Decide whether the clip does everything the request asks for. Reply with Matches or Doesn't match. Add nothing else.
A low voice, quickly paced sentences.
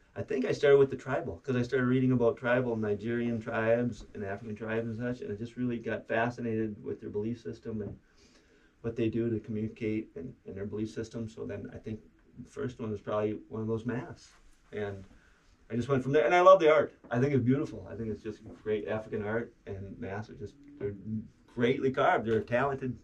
Matches